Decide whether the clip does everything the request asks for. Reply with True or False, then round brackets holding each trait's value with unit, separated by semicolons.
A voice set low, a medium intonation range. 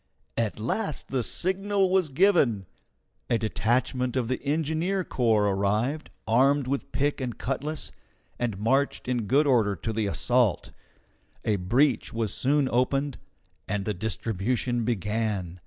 True (125 Hz; 4.6 semitones)